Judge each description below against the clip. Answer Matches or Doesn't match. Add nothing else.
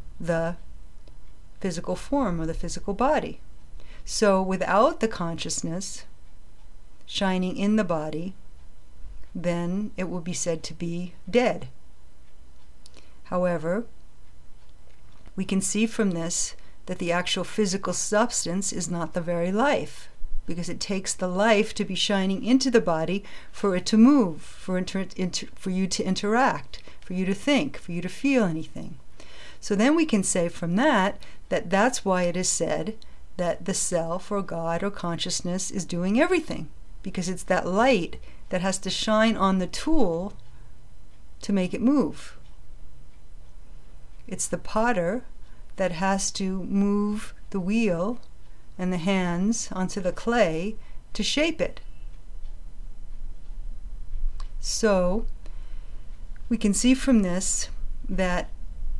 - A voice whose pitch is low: Doesn't match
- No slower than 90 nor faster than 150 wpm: Matches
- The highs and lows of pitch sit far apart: Doesn't match